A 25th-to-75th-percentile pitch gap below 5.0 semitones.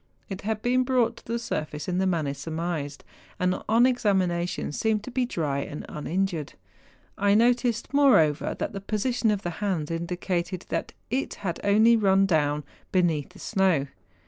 No: average, 5.3 semitones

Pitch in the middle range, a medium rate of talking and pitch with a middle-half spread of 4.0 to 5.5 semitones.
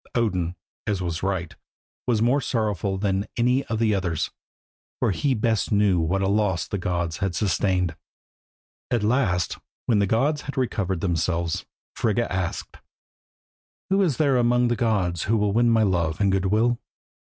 No: low, 100 Hz; average, 165 wpm; average, 4.4 semitones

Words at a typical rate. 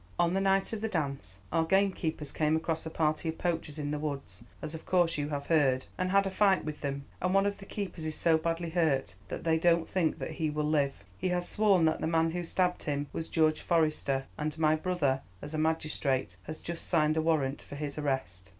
No: fast, 230 wpm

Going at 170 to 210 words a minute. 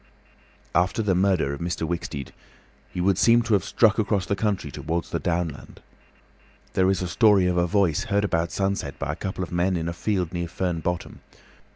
Yes: average, 200 wpm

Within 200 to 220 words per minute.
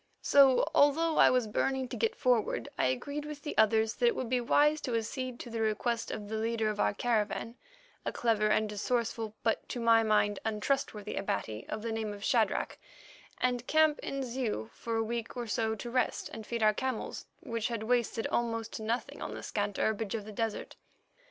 Yes: fast, 205 wpm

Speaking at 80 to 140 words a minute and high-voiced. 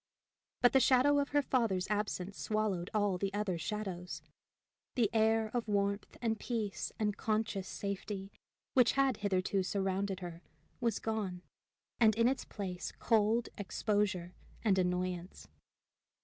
Yes: slow, 135 wpm; high, 205 Hz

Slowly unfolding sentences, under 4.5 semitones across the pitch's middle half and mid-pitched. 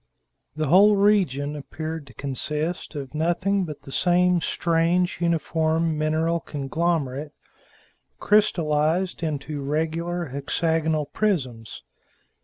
Yes: slow, 95 wpm; average, 2.8 semitones; medium, 160 Hz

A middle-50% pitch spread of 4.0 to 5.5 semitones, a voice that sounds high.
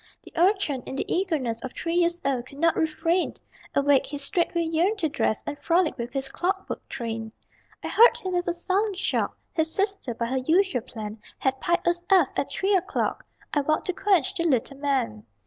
Yes: average, 5.2 semitones; very high, 320 Hz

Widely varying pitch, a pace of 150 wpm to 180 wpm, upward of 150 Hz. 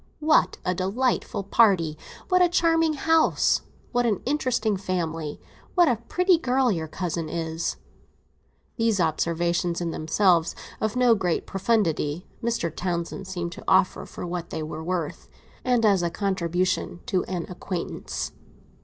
No: wide, 5.7 semitones; average, 140 wpm; medium, 185 Hz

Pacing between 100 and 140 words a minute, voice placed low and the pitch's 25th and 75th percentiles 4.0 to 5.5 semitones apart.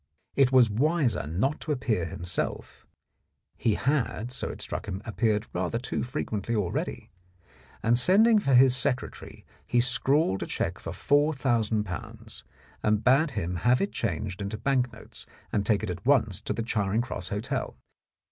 No: average, 160 wpm; low, 120 Hz; average, 4.5 semitones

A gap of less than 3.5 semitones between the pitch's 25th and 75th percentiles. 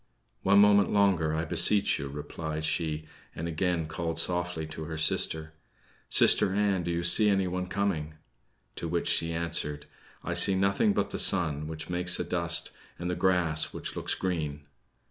Yes: average, 2.7 semitones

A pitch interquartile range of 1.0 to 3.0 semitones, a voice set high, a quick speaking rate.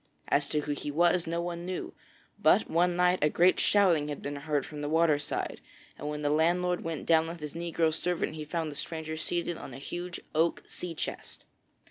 No: narrow, 2.5 semitones; medium, 165 Hz; fast, 210 wpm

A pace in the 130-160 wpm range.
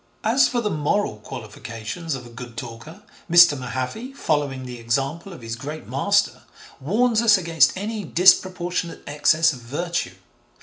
Yes: average, 145 wpm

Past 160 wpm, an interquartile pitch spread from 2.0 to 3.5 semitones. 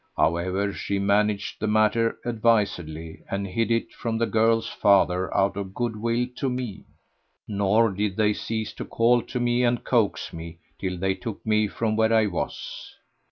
Yes: average, 170 wpm; average, 2.8 semitones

